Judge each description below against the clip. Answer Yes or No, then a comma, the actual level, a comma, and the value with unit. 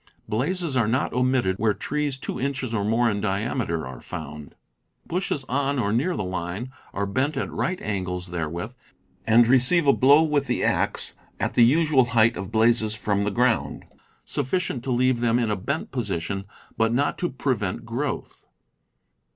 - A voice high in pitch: No, low, 120 Hz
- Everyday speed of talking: Yes, average, 170 wpm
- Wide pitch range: No, average, 4.8 semitones